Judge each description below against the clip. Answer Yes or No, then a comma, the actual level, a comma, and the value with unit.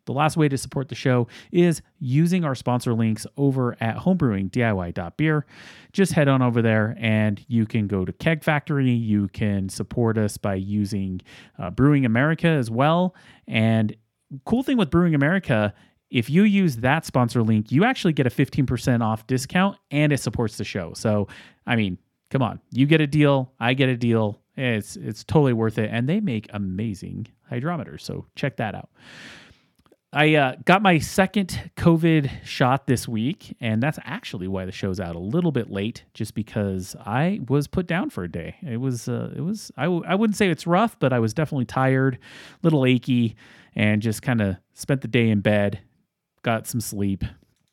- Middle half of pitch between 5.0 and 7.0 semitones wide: Yes, wide, 5.6 semitones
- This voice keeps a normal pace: Yes, average, 190 wpm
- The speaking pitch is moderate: No, low, 125 Hz